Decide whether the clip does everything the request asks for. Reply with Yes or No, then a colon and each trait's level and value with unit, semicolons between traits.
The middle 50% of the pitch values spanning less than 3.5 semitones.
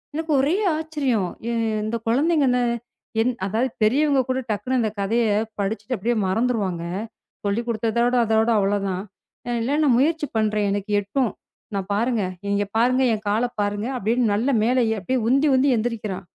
No: average, 3.8 semitones